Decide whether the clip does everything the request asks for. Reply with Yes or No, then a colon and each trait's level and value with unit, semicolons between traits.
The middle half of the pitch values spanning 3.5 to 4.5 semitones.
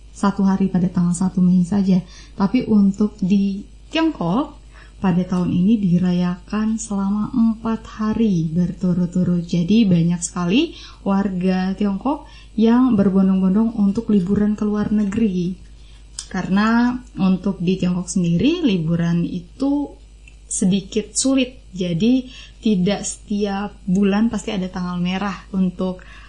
No: average, 3.1 semitones